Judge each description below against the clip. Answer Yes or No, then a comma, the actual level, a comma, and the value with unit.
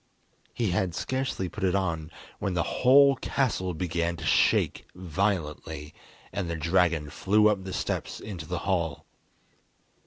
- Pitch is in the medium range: No, very low, 90 Hz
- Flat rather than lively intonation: No, average, 3.4 semitones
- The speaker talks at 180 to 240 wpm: No, average, 145 wpm